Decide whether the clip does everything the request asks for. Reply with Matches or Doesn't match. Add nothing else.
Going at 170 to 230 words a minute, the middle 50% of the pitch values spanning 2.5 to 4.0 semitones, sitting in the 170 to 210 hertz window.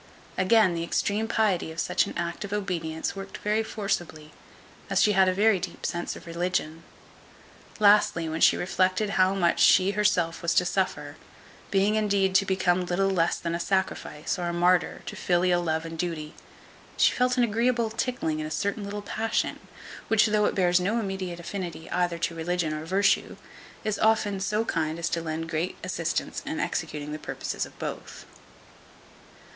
Matches